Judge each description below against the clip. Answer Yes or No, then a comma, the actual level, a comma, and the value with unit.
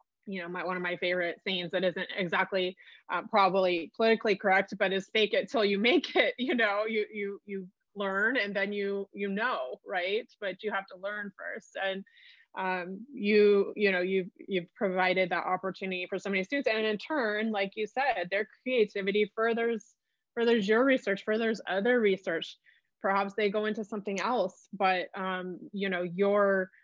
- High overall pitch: Yes, high, 200 Hz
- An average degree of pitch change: No, narrow, 2.2 semitones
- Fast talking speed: No, average, 180 wpm